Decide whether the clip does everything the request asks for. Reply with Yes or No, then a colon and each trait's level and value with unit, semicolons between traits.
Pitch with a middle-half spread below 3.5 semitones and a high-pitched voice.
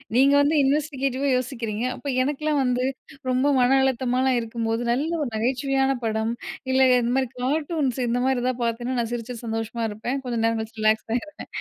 Yes: average, 2.7 semitones; very high, 250 Hz